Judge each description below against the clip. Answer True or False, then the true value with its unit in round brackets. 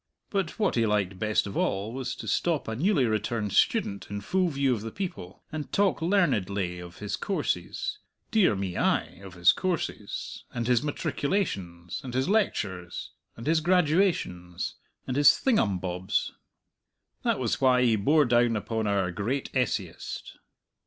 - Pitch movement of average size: False (8.1 semitones)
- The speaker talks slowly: False (155 wpm)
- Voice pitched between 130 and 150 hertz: False (115 Hz)